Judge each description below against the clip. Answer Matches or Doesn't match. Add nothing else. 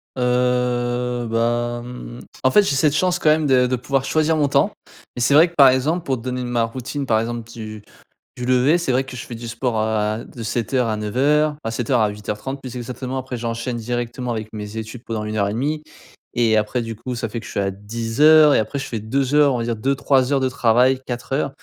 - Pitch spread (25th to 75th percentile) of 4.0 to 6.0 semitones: Doesn't match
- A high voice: Doesn't match